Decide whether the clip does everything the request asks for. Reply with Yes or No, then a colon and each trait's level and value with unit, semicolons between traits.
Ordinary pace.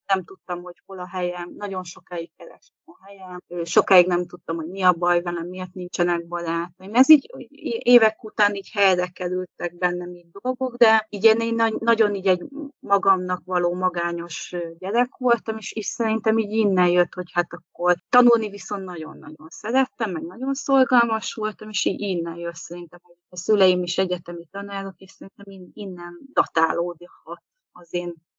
No: fast, 165 wpm